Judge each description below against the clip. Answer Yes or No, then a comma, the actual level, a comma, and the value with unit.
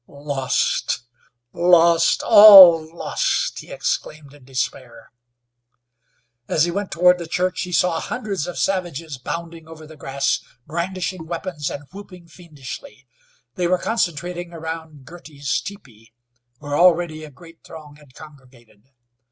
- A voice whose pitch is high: No, medium, 165 Hz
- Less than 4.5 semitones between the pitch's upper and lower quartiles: Yes, average, 3.6 semitones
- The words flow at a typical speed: No, slow, 125 wpm